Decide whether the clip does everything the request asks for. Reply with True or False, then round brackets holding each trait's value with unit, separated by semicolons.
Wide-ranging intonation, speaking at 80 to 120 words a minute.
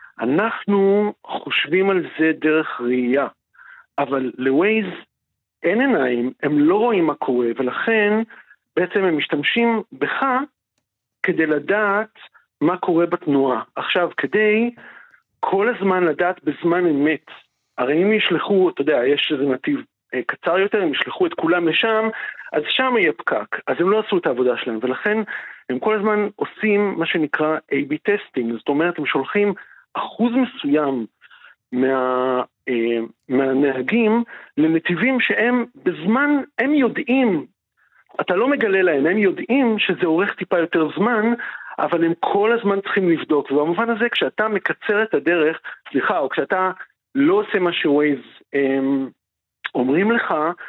False (7.5 semitones; 135 wpm)